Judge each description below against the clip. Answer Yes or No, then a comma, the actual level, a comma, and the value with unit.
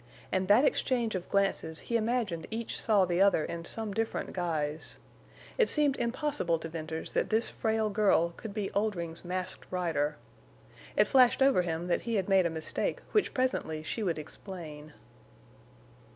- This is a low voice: No, high, 190 Hz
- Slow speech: No, average, 165 wpm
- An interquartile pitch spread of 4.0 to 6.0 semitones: Yes, average, 5.2 semitones